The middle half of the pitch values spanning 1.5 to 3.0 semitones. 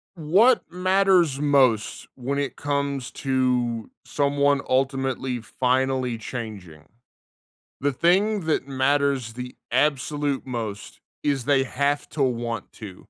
Yes: narrow, 2.6 semitones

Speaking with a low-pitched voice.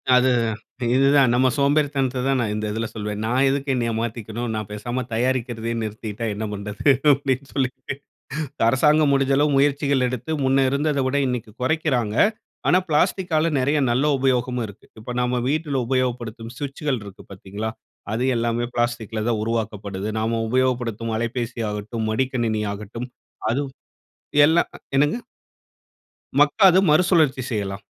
Yes: low, 125 Hz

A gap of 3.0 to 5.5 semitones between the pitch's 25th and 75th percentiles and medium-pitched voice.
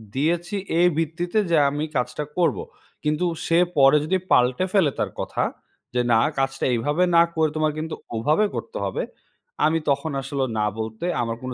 Yes: average, 4.4 semitones; medium, 150 Hz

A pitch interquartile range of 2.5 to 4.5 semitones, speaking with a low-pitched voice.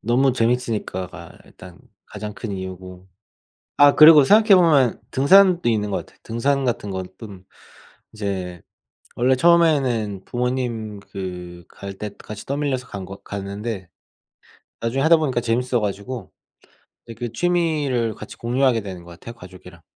No: average, 5.3 semitones; low, 115 Hz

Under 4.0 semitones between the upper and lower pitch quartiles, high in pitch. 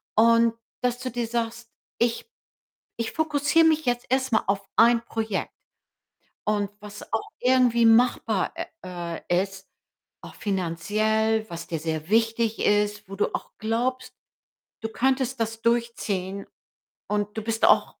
Yes: narrow, 2.6 semitones; high, 225 Hz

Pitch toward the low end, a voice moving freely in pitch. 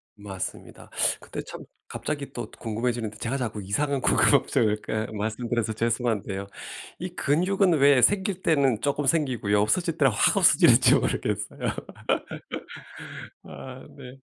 No: low, 125 Hz; average, 4.8 semitones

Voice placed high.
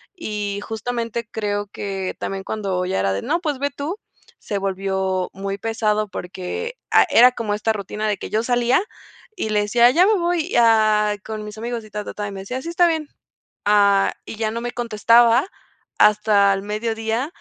Yes: high, 215 Hz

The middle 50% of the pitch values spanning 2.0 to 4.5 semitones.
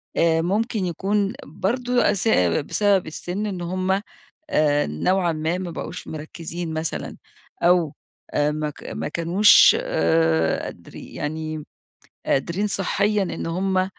Yes: average, 3.8 semitones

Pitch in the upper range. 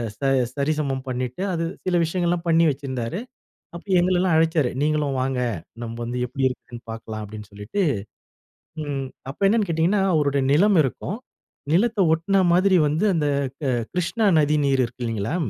No: medium, 150 Hz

